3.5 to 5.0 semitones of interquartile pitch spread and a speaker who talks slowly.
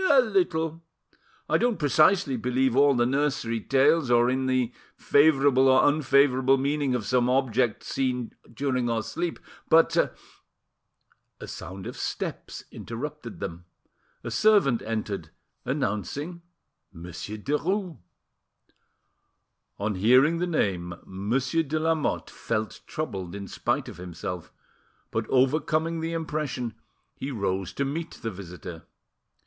No: wide, 5.6 semitones; slow, 120 wpm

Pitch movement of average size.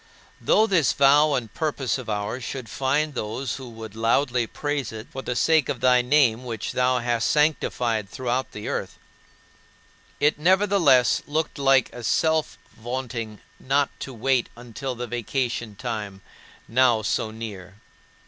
Yes: average, 3.5 semitones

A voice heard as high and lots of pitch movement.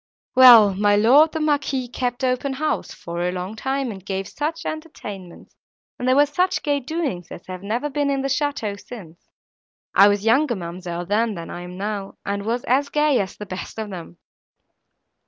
Yes: high, 225 Hz; wide, 6.3 semitones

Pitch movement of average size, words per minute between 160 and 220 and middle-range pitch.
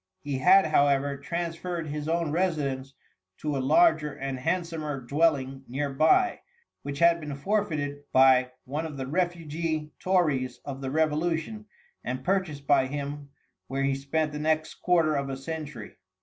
No: average, 3.3 semitones; average, 150 wpm; medium, 150 Hz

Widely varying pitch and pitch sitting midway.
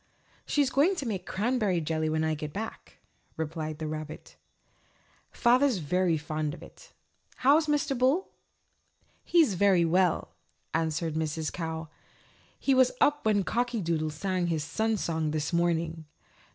Yes: wide, 7.2 semitones; medium, 175 Hz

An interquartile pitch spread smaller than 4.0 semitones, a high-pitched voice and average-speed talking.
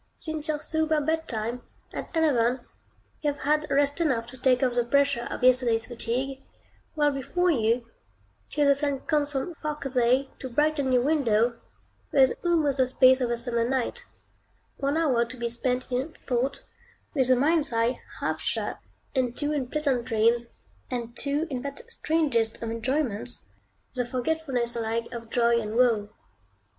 Yes: average, 3.6 semitones; very high, 260 Hz; average, 165 wpm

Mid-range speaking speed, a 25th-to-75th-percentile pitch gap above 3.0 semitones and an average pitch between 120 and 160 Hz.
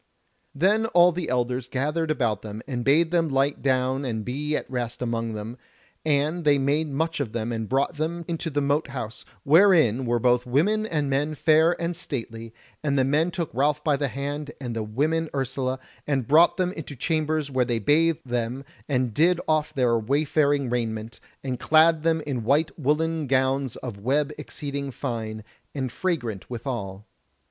Yes: average, 180 wpm; average, 4.2 semitones; medium, 140 Hz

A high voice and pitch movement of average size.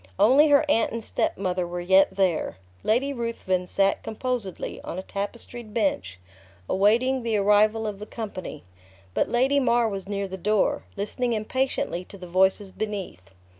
Yes: high, 210 Hz; average, 3.7 semitones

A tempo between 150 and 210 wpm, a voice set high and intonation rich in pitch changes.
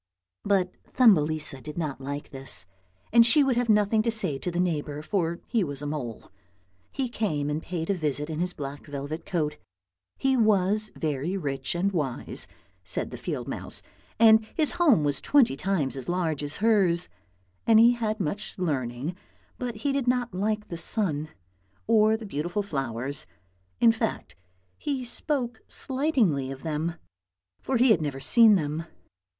No: average, 165 wpm; medium, 180 Hz; wide, 7.0 semitones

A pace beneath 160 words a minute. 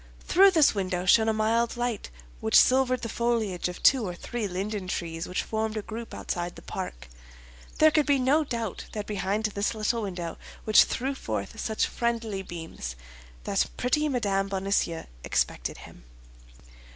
No: average, 165 wpm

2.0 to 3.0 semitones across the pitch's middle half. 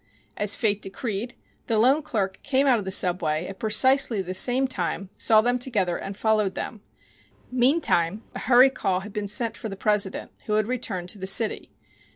No: average, 4.1 semitones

